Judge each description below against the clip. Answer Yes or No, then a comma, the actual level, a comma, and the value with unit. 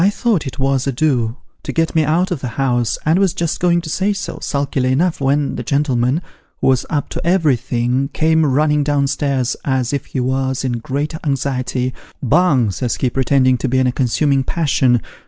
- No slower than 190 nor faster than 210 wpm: Yes, fast, 205 wpm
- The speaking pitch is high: No, low, 135 Hz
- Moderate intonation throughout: Yes, average, 3.4 semitones